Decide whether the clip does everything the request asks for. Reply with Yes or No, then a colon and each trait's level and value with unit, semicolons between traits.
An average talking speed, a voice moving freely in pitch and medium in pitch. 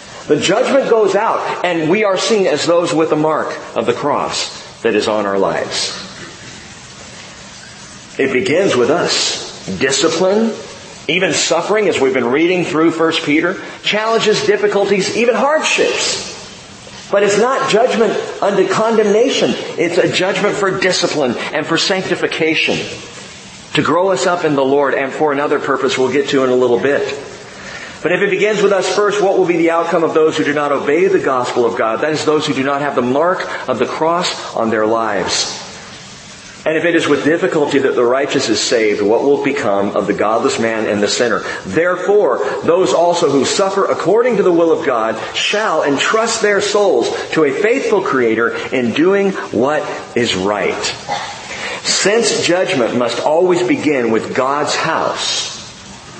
Yes: average, 170 wpm; wide, 5.8 semitones; medium, 175 Hz